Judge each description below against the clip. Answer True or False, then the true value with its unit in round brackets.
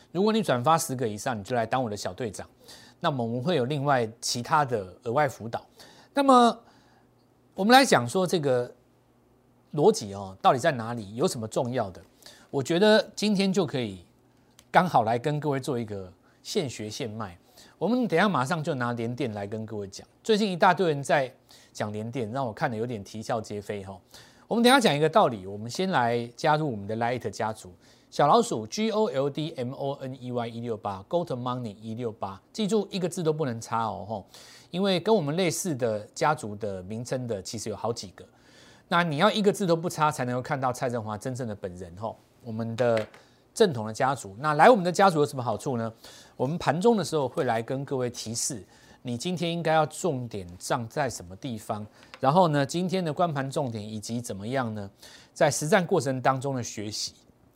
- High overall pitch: False (130 Hz)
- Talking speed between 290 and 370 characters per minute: True (310 characters per minute)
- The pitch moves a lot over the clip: True (6.7 semitones)